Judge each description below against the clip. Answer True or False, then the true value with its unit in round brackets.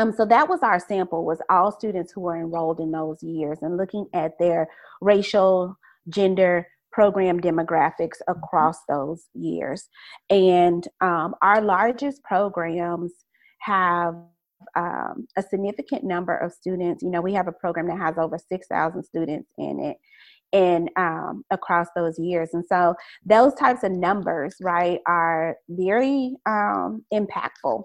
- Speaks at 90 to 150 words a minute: True (145 wpm)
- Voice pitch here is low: False (180 Hz)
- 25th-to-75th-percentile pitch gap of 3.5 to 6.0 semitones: False (3.1 semitones)